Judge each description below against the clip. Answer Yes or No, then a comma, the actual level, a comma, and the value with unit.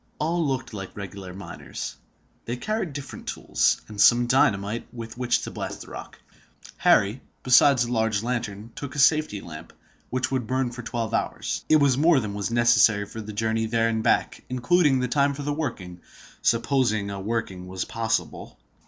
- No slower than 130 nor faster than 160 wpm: No, average, 175 wpm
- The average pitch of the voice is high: No, low, 115 Hz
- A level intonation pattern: No, average, 4.3 semitones